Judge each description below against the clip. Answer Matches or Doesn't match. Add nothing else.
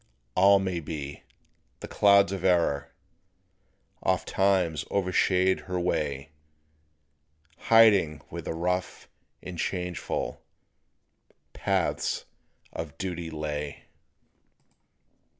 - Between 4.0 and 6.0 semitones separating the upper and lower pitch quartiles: Doesn't match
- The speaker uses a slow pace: Matches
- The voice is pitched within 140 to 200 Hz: Doesn't match